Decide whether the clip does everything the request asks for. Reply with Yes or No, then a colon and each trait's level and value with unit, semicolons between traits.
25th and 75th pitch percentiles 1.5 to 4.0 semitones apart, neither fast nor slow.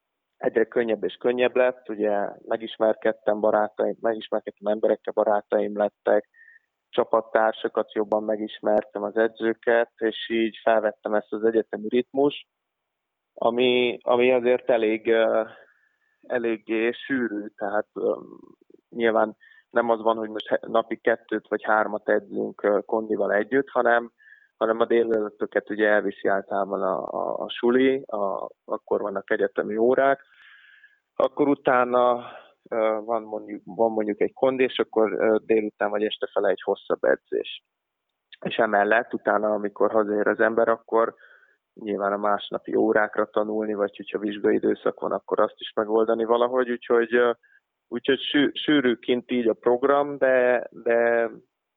Yes: narrow, 2.6 semitones; average, 125 wpm